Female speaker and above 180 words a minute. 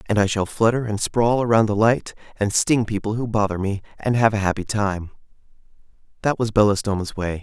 No: male; average, 195 wpm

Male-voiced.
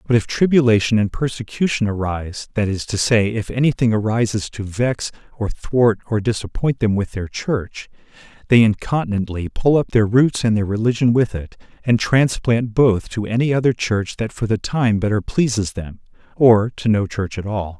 Yes: male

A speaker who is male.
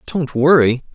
Yes: male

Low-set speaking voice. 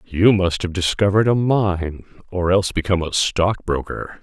Yes: very low, 95 Hz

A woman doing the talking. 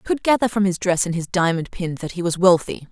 Yes: female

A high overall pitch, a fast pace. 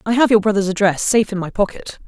Yes: high, 205 Hz; fast, 260 wpm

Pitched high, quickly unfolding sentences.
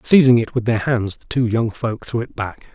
No: low, 115 Hz; fast, 260 wpm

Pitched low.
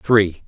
Yes: very low, 95 Hz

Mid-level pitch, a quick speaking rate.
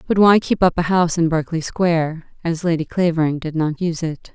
Yes: medium, 165 Hz; fast, 220 wpm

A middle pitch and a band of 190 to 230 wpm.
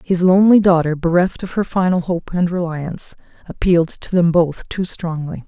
No: medium, 175 Hz; average, 175 wpm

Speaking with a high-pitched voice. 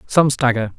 No: low, 125 Hz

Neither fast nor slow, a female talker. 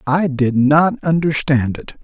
No: average, 145 wpm; male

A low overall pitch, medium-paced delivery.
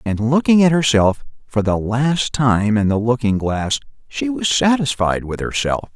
Yes: low, 125 Hz; average, 170 wpm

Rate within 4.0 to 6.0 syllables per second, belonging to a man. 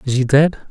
No: 6.7 syllables/s; male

